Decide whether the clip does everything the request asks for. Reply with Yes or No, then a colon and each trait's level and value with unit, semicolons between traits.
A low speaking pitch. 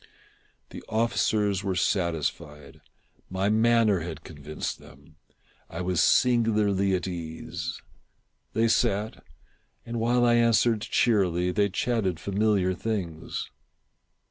Yes: low, 100 Hz